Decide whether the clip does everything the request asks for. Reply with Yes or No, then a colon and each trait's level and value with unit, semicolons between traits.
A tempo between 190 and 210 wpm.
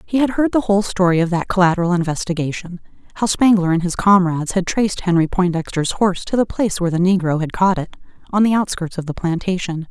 Yes: average, 200 wpm